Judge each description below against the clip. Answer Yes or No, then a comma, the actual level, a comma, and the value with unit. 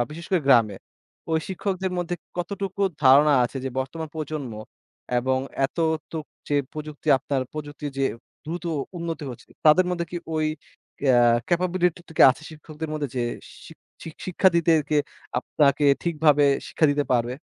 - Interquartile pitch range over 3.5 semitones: No, average, 3.0 semitones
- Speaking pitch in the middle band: Yes, medium, 155 Hz